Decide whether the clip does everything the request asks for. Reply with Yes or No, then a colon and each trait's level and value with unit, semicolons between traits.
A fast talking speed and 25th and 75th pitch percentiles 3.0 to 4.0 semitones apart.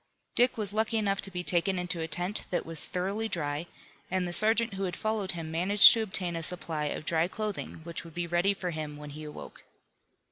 Yes: fast, 220 wpm; average, 3.6 semitones